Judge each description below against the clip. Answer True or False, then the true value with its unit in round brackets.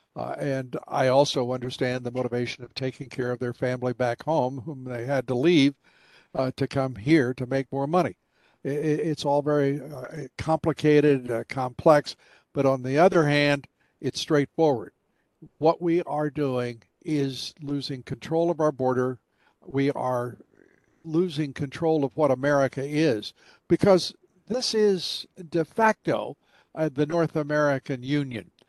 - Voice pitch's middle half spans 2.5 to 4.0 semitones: True (3.5 semitones)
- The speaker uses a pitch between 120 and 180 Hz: True (140 Hz)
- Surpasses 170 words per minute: False (150 wpm)